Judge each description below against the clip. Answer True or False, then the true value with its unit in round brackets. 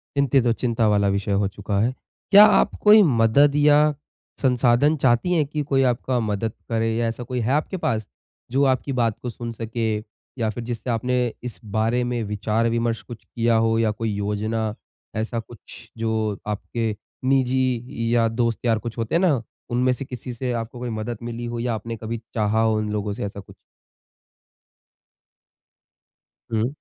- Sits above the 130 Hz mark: False (115 Hz)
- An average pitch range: False (2.3 semitones)